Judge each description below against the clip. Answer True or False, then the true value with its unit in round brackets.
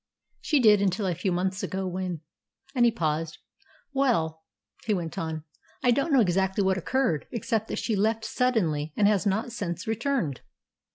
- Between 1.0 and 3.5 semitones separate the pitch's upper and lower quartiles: False (5.0 semitones)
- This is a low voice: False (195 Hz)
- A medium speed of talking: True (175 wpm)